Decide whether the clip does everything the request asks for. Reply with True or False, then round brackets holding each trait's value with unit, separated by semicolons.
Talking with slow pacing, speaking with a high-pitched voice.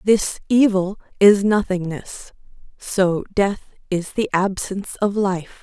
True (115 wpm; 195 Hz)